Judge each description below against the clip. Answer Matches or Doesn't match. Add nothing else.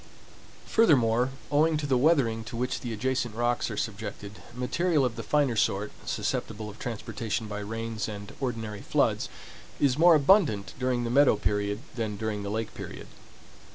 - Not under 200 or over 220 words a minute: Doesn't match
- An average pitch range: Matches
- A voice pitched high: Doesn't match